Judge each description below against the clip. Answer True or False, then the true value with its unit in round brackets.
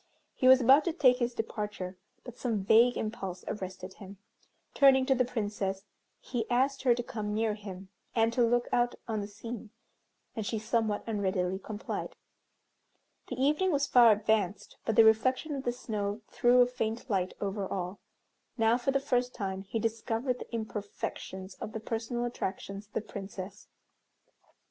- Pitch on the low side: False (225 Hz)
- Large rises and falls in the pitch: False (3.4 semitones)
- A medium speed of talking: True (170 wpm)